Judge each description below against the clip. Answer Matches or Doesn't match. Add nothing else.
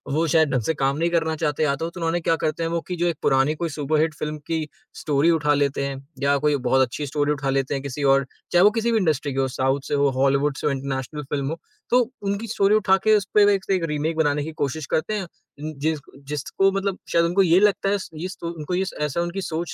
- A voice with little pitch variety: Doesn't match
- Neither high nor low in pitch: Matches